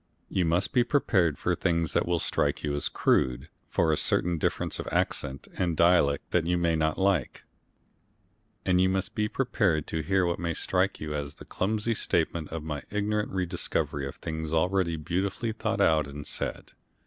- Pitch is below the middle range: Yes, very low, 85 Hz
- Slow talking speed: No, average, 185 wpm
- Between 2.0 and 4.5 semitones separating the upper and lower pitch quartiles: Yes, average, 3.5 semitones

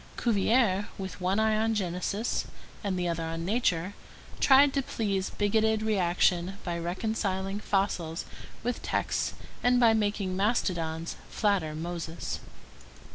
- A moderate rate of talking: No, slow, 125 wpm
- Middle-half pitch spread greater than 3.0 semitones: Yes, average, 3.8 semitones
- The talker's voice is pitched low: No, high, 195 Hz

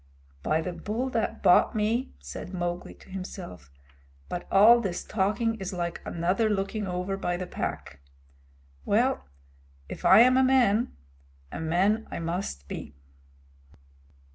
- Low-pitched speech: No, high, 190 Hz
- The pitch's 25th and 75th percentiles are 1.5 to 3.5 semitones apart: No, average, 4.0 semitones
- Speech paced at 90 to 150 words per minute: Yes, average, 140 wpm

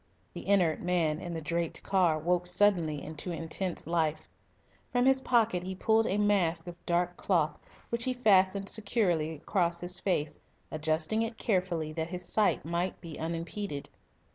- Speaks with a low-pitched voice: No, medium, 175 Hz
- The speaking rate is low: No, average, 160 wpm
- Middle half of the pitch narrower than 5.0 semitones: Yes, average, 3.6 semitones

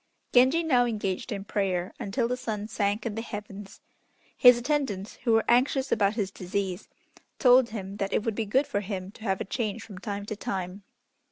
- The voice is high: Yes, high, 210 Hz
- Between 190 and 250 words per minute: Yes, average, 195 wpm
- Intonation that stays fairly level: No, average, 3.5 semitones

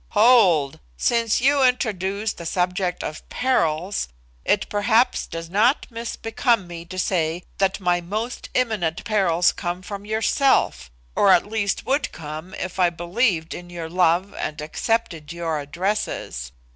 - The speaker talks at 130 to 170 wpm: Yes, average, 140 wpm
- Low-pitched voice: No, medium, 185 Hz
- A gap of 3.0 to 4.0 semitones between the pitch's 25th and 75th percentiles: No, average, 4.5 semitones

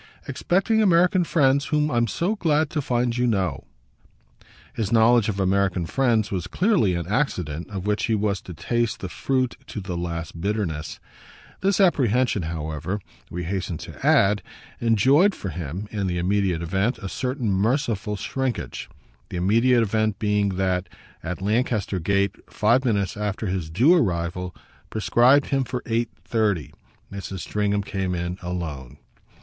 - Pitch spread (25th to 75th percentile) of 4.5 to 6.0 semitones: Yes, average, 5.3 semitones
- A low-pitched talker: Yes, low, 105 Hz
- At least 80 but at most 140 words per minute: No, average, 150 wpm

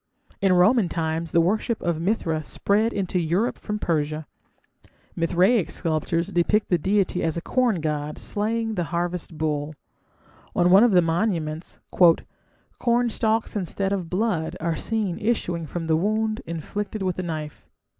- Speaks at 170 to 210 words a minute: No, average, 145 wpm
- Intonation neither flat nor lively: Yes, average, 4.5 semitones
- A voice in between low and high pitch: Yes, medium, 180 Hz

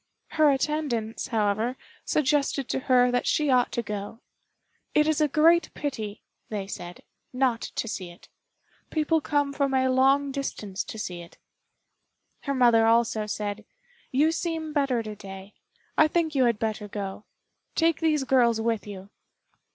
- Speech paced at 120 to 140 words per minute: No, average, 155 wpm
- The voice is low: No, very high, 250 Hz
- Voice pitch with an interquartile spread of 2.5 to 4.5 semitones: No, average, 5.3 semitones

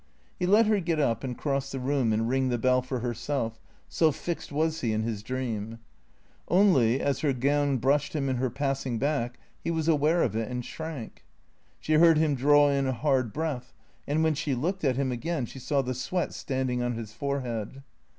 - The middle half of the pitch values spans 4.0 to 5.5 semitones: No, average, 3.6 semitones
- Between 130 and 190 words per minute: No, fast, 205 wpm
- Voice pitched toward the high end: No, low, 135 Hz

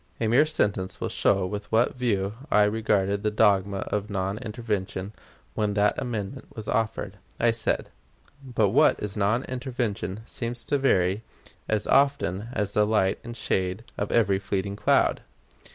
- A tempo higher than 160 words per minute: No, average, 155 wpm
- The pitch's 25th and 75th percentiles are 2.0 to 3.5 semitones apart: Yes, average, 2.8 semitones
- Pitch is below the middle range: Yes, low, 105 Hz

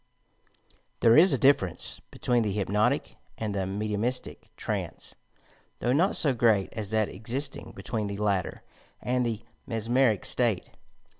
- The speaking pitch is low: Yes, low, 110 Hz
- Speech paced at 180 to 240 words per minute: No, average, 140 wpm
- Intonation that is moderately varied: Yes, average, 3.3 semitones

